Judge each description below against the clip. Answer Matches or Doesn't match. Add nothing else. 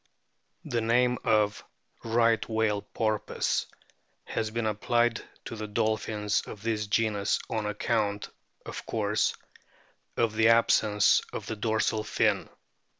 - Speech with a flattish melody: Matches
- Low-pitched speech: Matches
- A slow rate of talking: Matches